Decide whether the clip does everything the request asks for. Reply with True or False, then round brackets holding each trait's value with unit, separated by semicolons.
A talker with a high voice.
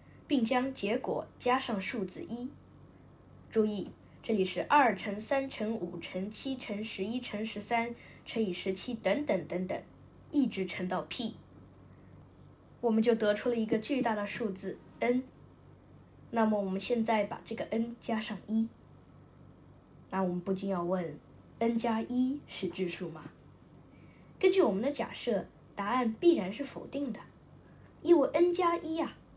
True (225 Hz)